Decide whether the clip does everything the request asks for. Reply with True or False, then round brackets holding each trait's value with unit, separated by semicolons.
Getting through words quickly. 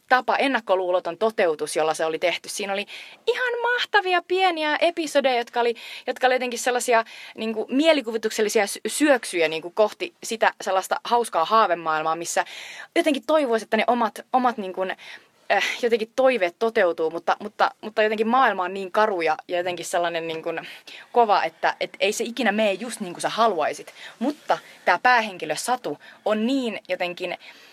True (160 wpm)